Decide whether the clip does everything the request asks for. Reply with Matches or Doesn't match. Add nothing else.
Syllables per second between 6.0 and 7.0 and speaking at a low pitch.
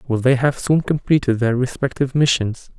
Doesn't match